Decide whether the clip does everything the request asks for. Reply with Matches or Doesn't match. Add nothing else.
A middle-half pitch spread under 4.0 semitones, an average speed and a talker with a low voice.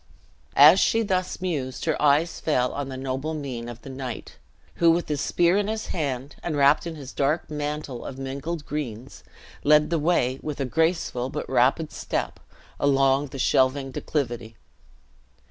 Doesn't match